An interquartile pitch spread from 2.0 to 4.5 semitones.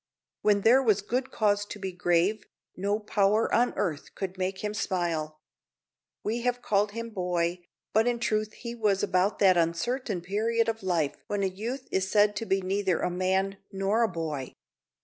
Yes: average, 3.2 semitones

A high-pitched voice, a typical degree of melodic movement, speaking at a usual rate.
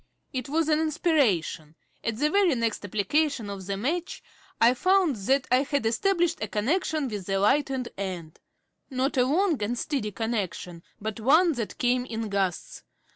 No: very high, 250 Hz; wide, 6.6 semitones; average, 165 wpm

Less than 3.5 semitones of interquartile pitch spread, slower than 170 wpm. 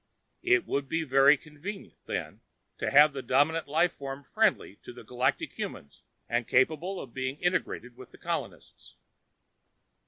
No: average, 4.1 semitones; average, 150 wpm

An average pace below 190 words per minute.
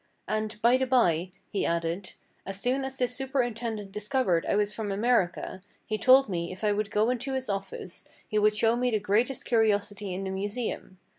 No: average, 195 wpm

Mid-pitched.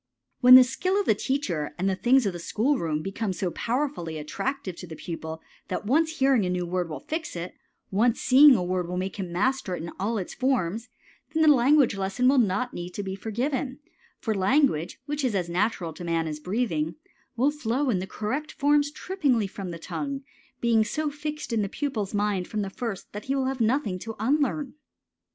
No: high, 220 Hz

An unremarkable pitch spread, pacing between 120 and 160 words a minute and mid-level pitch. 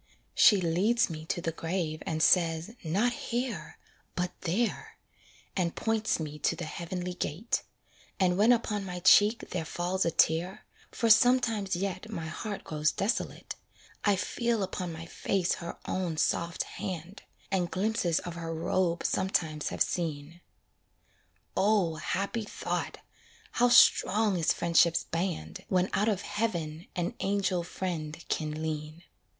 Yes: average, 3.8 semitones; average, 140 wpm; medium, 180 Hz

